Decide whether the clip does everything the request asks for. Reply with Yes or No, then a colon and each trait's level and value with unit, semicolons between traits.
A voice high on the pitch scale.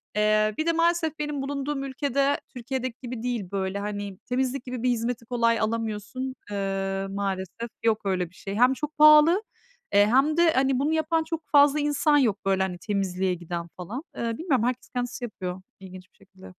Yes: high, 240 Hz